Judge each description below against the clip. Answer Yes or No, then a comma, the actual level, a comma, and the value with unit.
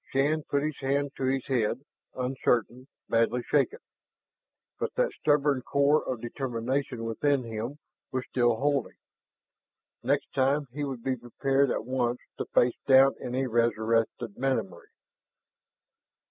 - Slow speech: Yes, slow, 130 wpm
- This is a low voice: Yes, low, 130 Hz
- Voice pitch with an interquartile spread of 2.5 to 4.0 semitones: Yes, average, 2.8 semitones